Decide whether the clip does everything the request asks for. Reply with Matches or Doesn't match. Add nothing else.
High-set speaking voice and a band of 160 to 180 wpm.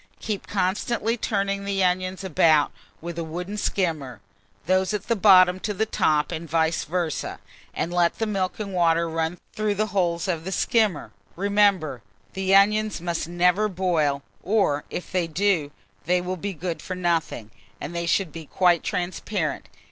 Doesn't match